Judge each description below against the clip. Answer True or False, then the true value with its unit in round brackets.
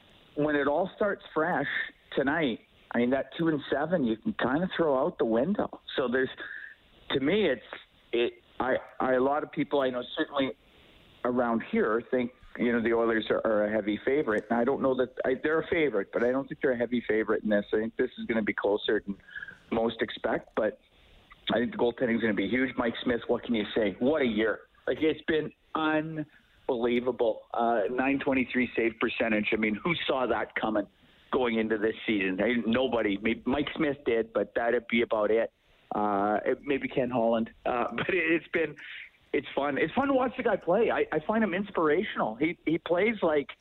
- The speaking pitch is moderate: False (125 Hz)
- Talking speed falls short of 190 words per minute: False (205 wpm)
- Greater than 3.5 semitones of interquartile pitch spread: True (4.7 semitones)